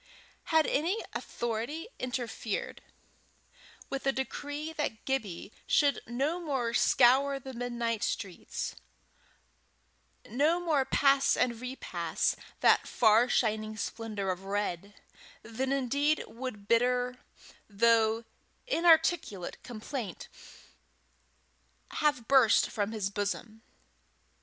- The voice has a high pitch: Yes, high, 245 Hz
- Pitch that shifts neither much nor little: Yes, average, 4.1 semitones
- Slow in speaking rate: Yes, slow, 95 wpm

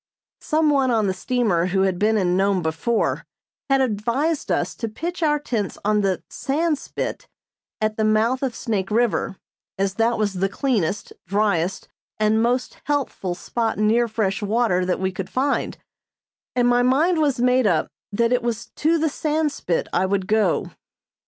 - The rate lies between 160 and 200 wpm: Yes, average, 165 wpm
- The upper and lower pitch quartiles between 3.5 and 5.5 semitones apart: Yes, average, 4.8 semitones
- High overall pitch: Yes, high, 220 Hz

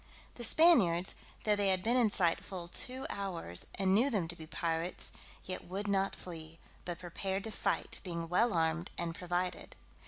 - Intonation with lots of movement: No, average, 3.1 semitones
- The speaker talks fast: No, average, 180 wpm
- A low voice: No, medium, 185 Hz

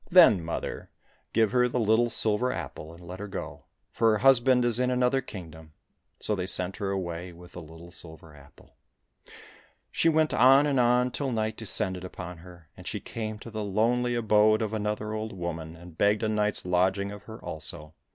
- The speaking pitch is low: Yes, low, 105 Hz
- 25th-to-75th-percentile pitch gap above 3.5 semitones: Yes, average, 5.1 semitones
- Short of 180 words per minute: No, average, 200 wpm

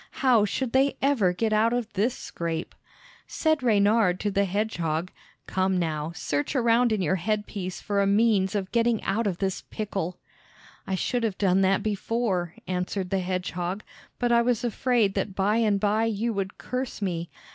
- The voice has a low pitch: No, high, 205 Hz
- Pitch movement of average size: Yes, average, 3.7 semitones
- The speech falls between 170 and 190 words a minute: Yes, average, 180 wpm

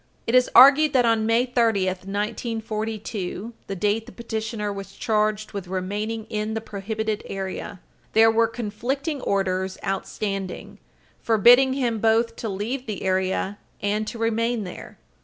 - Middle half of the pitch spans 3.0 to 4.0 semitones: No, narrow, 2.5 semitones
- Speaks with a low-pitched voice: No, high, 220 Hz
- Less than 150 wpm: Yes, average, 140 wpm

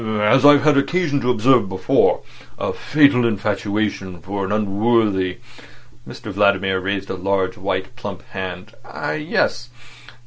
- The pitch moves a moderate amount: Yes, average, 4.4 semitones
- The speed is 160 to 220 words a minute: No, slow, 135 wpm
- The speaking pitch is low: Yes, low, 105 Hz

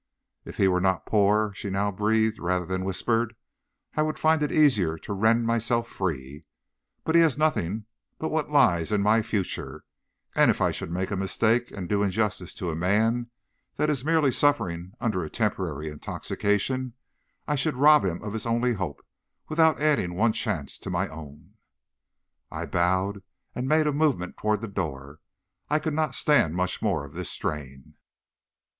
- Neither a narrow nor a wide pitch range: No, wide, 6.1 semitones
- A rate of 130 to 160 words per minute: No, average, 175 wpm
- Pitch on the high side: No, low, 105 Hz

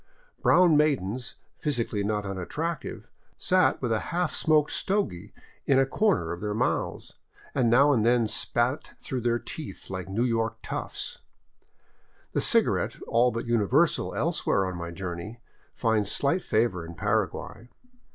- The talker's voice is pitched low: Yes, low, 120 Hz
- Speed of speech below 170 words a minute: Yes, average, 140 wpm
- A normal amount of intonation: No, wide, 6.1 semitones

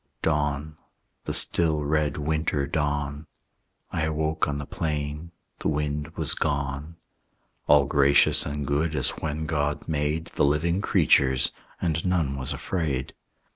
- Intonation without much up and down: Yes, narrow, 1.5 semitones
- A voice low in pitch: Yes, very low, 75 Hz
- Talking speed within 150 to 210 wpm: No, slow, 135 wpm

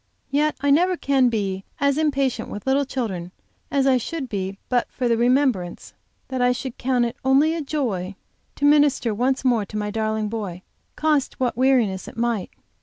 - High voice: Yes, very high, 250 Hz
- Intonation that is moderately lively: Yes, average, 4.4 semitones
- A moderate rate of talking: Yes, average, 180 wpm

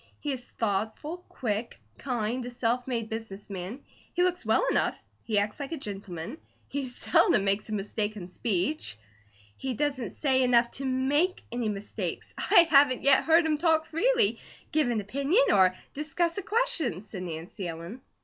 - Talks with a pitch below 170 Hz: No, high, 245 Hz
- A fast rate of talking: No, average, 170 wpm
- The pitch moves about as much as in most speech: No, wide, 6.5 semitones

